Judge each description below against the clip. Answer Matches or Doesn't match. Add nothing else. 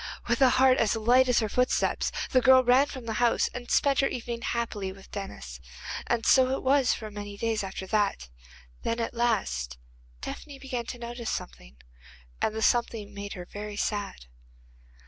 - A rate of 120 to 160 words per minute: Doesn't match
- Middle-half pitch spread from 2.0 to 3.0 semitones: Doesn't match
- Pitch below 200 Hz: Doesn't match